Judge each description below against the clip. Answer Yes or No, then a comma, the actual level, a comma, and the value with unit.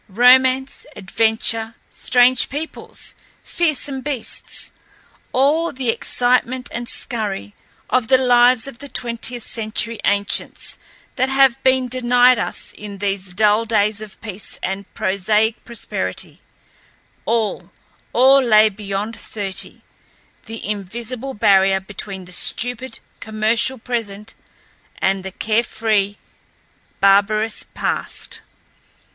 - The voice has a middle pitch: No, high, 225 Hz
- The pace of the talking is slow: Yes, slow, 100 wpm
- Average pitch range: Yes, average, 3.6 semitones